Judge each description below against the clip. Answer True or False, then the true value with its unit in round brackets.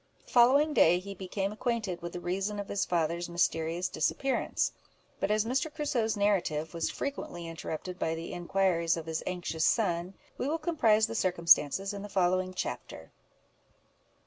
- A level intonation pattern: False (4.1 semitones)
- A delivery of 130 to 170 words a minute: True (160 wpm)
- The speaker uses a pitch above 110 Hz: True (185 Hz)